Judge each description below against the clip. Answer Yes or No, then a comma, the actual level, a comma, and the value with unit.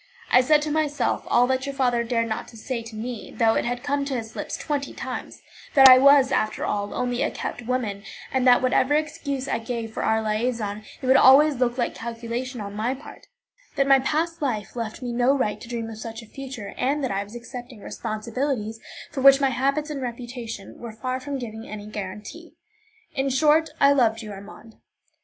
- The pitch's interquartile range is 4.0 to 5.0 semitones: No, average, 3.4 semitones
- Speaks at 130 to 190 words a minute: No, fast, 205 wpm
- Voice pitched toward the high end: Yes, high, 245 Hz